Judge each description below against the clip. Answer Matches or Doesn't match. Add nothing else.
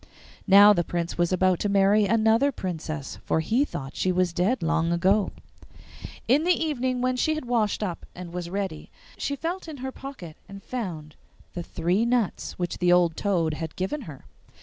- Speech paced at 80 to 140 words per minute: Doesn't match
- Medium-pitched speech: Doesn't match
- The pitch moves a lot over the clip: Matches